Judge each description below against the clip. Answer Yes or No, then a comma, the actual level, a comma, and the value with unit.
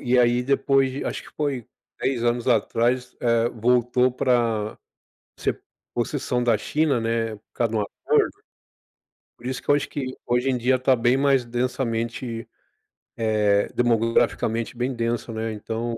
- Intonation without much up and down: Yes, narrow, 1.9 semitones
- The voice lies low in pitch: Yes, low, 120 Hz